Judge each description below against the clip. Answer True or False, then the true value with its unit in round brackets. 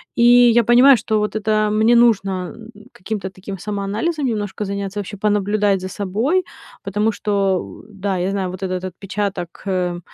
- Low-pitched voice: False (205 Hz)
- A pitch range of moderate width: False (2.2 semitones)